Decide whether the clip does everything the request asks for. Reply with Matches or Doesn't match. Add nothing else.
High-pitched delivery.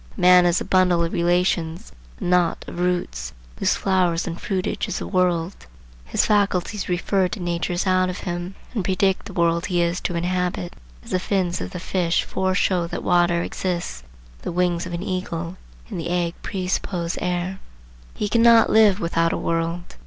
Doesn't match